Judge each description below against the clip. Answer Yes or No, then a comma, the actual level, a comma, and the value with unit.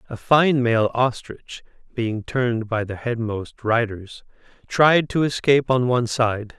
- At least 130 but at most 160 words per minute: Yes, average, 145 wpm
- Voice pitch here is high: No, low, 120 Hz